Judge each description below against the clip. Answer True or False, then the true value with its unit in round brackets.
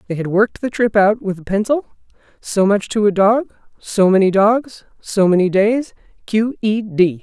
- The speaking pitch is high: True (210 Hz)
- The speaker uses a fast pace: False (190 wpm)